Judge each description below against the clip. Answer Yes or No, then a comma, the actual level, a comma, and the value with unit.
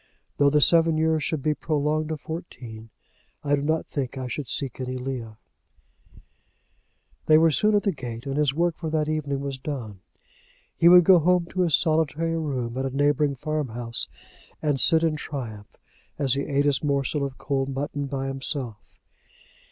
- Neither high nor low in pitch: Yes, medium, 145 Hz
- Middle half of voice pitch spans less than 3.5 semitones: Yes, average, 2.9 semitones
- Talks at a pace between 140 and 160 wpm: No, average, 180 wpm